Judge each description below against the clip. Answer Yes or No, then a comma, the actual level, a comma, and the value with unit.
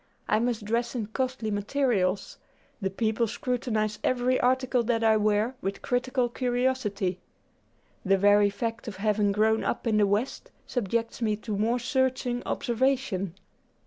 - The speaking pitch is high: Yes, high, 225 Hz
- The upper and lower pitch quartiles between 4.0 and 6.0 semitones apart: No, average, 3.1 semitones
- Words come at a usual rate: Yes, average, 145 wpm